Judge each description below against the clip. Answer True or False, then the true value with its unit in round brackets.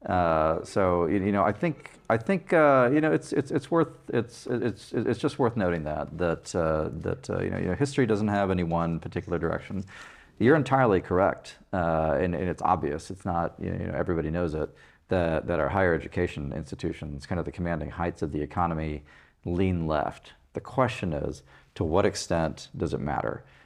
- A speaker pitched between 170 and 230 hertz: False (85 Hz)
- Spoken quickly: False (195 wpm)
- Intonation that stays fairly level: False (4.7 semitones)